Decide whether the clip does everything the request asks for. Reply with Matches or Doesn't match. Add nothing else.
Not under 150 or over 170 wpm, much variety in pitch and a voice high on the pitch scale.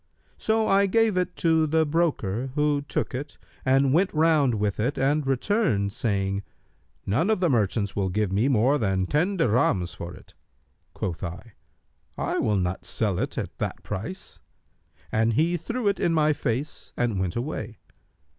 Doesn't match